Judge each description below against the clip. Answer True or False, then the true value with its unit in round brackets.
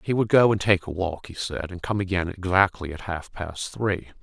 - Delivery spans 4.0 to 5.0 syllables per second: False (5.2 syllables/s)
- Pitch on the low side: True (95 Hz)